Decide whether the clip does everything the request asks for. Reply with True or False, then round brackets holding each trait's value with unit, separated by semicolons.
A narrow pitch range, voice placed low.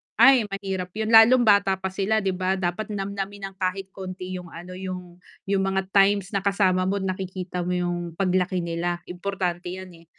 False (1.5 semitones; 190 Hz)